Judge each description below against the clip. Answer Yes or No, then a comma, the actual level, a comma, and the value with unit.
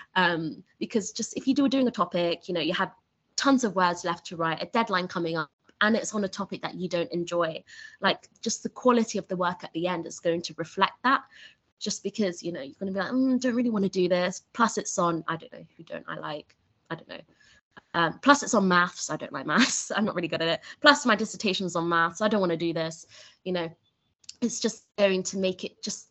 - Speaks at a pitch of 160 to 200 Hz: Yes, high, 190 Hz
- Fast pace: Yes, fast, 260 wpm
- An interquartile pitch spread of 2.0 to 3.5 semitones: No, average, 4.5 semitones